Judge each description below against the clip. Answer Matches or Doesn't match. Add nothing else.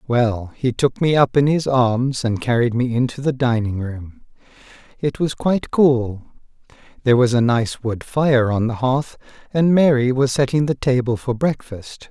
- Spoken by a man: Matches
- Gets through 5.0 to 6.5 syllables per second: Doesn't match